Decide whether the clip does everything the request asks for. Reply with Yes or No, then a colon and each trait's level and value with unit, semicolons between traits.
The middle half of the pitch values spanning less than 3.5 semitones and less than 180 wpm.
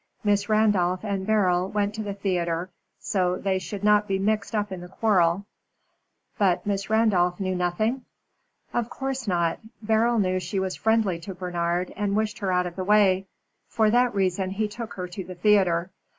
No: average, 2.8 semitones; average, 185 wpm